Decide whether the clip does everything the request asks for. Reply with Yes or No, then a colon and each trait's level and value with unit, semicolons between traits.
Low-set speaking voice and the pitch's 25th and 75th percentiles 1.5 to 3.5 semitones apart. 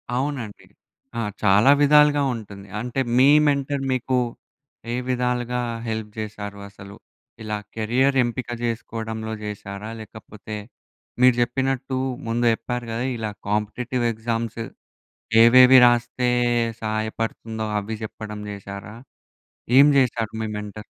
Yes: low, 115 Hz; average, 2.8 semitones